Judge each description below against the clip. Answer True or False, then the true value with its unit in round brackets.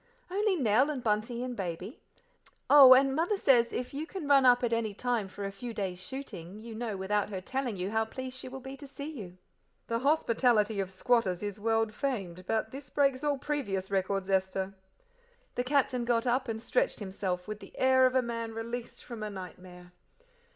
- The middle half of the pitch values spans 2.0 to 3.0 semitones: False (4.8 semitones)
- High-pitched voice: True (230 Hz)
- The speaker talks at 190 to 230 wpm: True (200 wpm)